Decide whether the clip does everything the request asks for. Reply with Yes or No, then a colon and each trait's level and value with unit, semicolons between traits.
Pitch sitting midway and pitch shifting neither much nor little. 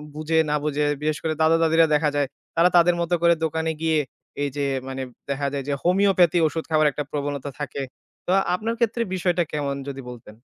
Yes: medium, 155 Hz; average, 3.0 semitones